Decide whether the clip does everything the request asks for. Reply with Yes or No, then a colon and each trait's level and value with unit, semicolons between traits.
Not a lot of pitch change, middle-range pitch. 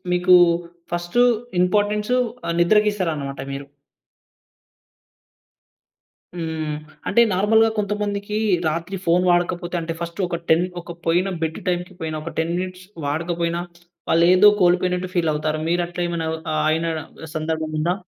Yes: narrow, 2.2 semitones; medium, 175 Hz